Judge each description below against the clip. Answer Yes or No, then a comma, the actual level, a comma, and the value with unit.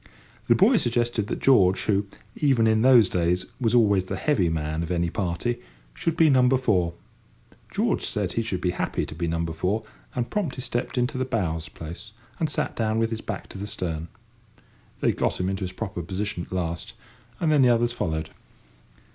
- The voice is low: Yes, low, 105 Hz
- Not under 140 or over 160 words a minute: No, average, 190 wpm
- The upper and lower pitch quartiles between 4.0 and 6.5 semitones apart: Yes, wide, 5.5 semitones